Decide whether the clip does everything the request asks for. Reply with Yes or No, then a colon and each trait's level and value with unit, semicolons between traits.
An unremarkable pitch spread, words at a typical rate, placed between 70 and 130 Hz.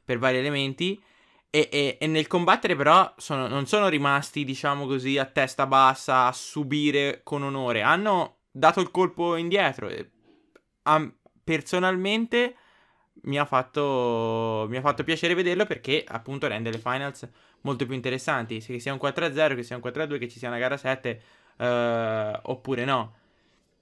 No: average, 3.7 semitones; average, 160 wpm; medium, 140 Hz